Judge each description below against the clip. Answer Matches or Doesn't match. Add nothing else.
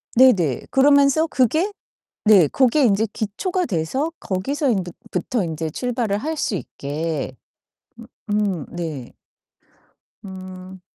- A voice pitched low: Doesn't match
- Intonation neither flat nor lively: Doesn't match